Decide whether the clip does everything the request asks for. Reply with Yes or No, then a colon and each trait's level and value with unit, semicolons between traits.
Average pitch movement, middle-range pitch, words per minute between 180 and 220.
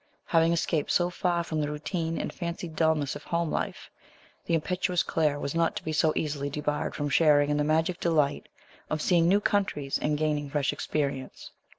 No: narrow, 2.3 semitones; medium, 155 Hz; average, 190 wpm